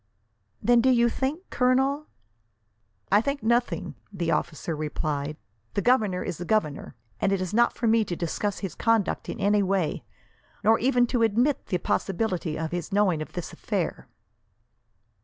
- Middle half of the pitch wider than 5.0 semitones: Yes, wide, 5.6 semitones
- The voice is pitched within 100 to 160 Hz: No, high, 205 Hz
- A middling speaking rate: Yes, average, 165 wpm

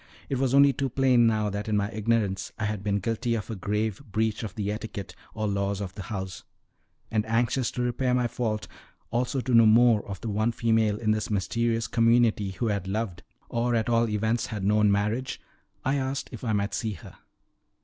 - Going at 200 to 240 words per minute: Yes, fast, 205 wpm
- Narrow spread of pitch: Yes, narrow, 2.3 semitones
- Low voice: Yes, low, 110 Hz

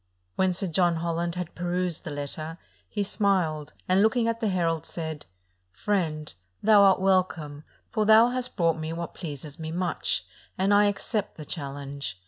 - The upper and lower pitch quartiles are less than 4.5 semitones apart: Yes, average, 4.1 semitones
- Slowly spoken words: No, average, 165 wpm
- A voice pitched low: No, medium, 175 Hz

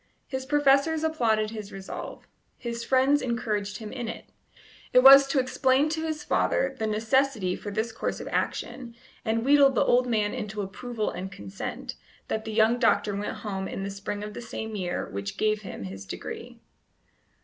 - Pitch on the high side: Yes, high, 225 Hz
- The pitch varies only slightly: No, average, 4.2 semitones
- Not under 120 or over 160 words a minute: No, average, 180 wpm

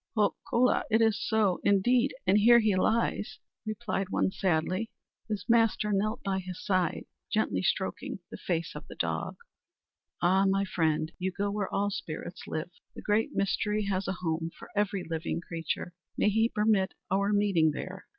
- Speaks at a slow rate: No, average, 170 wpm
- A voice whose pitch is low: No, high, 195 Hz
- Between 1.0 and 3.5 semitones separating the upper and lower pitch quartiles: Yes, average, 2.7 semitones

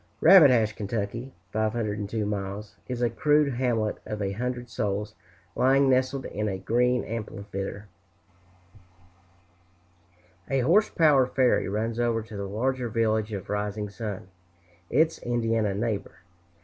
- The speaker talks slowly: Yes, slow, 125 wpm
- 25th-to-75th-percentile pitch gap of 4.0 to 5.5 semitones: No, average, 3.3 semitones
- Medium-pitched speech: No, low, 115 Hz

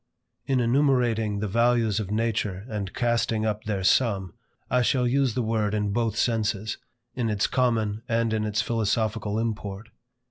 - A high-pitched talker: No, low, 110 Hz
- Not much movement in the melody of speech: Yes, narrow, 2.2 semitones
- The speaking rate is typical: Yes, average, 155 wpm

